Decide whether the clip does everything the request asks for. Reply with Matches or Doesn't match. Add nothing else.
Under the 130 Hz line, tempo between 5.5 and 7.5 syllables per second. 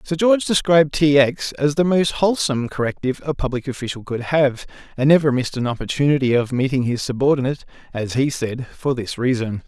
Doesn't match